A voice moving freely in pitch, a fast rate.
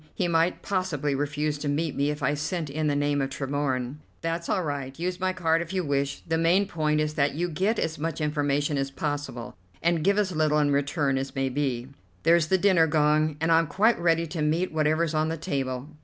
No: narrow, 2.6 semitones; fast, 220 wpm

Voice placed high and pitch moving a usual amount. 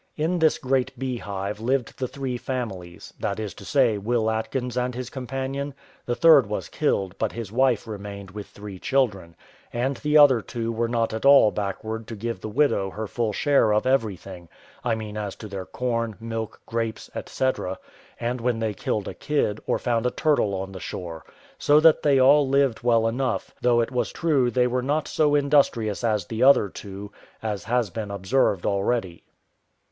No: low, 115 Hz; average, 4.1 semitones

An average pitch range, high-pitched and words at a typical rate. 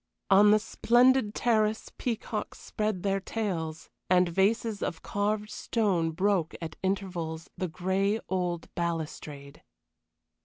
No: average, 3.9 semitones; high, 195 Hz; slow, 115 wpm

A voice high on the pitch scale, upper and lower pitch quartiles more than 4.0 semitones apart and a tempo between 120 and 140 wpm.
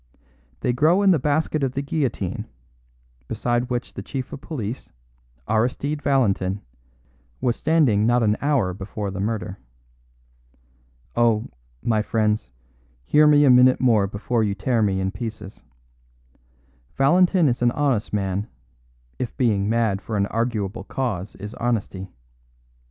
No: low, 115 Hz; average, 4.6 semitones; slow, 135 wpm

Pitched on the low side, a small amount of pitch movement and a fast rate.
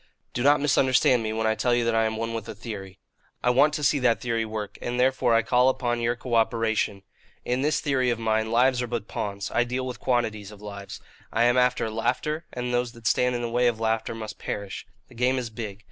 Yes: low, 120 Hz; narrow, 2.2 semitones; fast, 240 wpm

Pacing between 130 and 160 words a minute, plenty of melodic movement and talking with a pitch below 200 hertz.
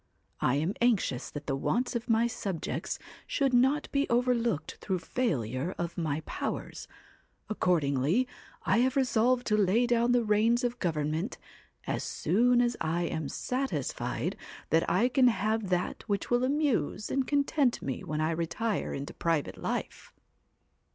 No: average, 150 wpm; wide, 6.8 semitones; high, 220 Hz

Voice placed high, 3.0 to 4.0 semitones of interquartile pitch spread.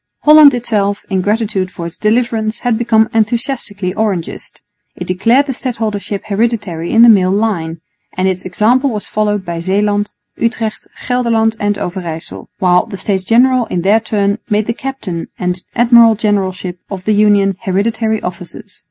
Yes: high, 210 Hz; average, 3.5 semitones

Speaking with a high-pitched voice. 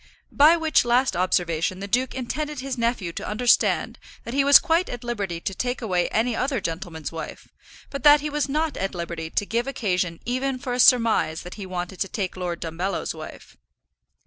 Yes: high, 230 Hz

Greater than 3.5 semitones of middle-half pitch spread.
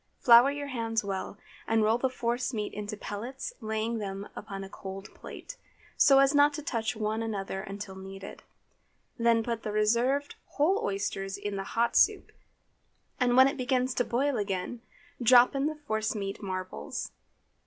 Yes: average, 4.2 semitones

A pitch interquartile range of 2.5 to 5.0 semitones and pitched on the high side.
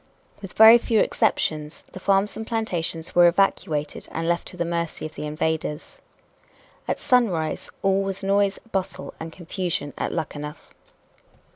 No: average, 3.7 semitones; medium, 175 Hz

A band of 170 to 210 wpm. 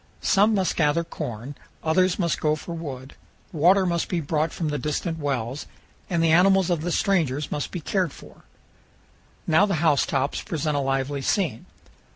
Yes: average, 175 wpm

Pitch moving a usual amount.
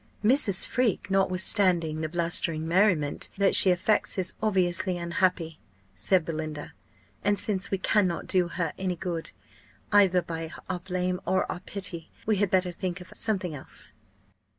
No: narrow, 2.3 semitones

